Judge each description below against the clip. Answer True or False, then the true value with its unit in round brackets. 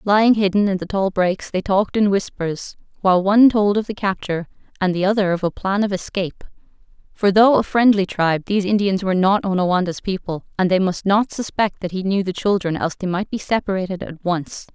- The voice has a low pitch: False (195 Hz)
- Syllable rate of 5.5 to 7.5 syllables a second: True (6.0 syllables/s)